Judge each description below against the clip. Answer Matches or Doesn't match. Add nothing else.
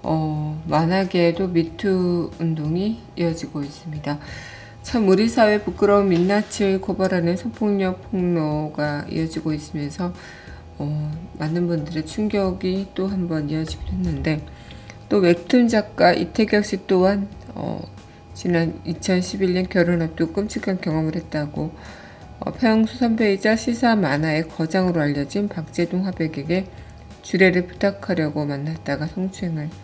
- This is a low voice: Doesn't match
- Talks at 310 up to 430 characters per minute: Doesn't match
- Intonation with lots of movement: Doesn't match